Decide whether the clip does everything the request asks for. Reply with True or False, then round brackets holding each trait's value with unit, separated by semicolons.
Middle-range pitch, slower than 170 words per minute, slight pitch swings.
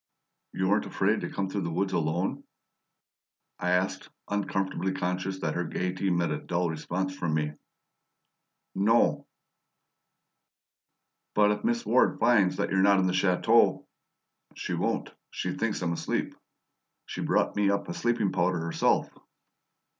False (95 Hz; 145 wpm; 2.3 semitones)